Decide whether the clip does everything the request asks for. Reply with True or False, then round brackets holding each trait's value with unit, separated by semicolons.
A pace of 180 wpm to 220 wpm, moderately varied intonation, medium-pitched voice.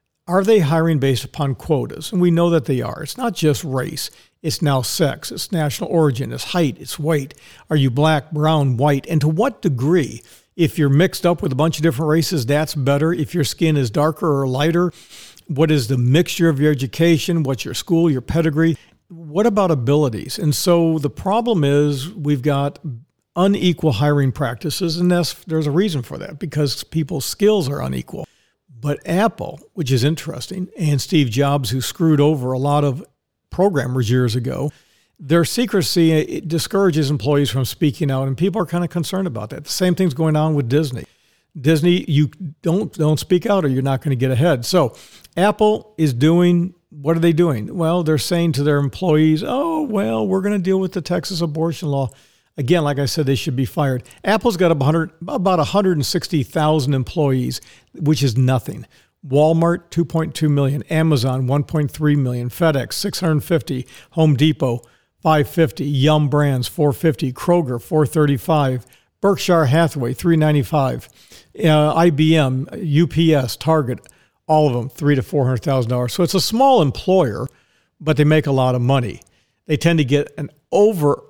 True (185 wpm; 3.5 semitones; 155 Hz)